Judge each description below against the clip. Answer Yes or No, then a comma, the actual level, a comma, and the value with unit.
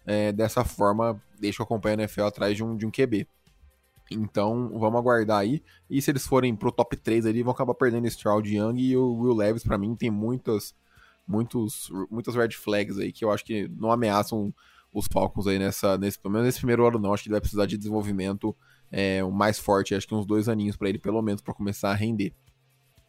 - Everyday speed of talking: No, fast, 225 wpm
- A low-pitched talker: Yes, low, 110 Hz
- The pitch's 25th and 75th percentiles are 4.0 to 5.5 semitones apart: No, narrow, 2.5 semitones